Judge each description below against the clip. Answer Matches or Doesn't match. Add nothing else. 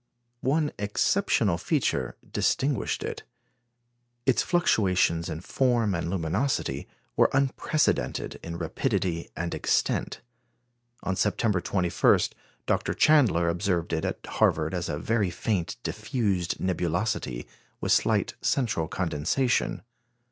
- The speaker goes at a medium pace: Doesn't match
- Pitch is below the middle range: Matches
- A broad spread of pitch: Matches